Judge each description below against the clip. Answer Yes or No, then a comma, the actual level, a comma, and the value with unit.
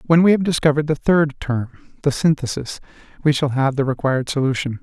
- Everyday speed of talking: Yes, average, 185 wpm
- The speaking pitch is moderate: Yes, medium, 145 Hz